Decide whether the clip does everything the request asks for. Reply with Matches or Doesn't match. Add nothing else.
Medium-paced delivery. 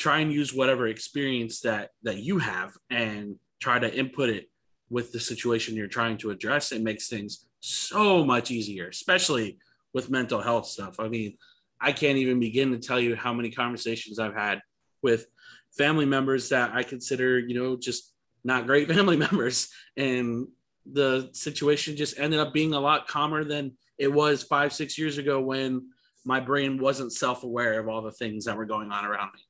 Matches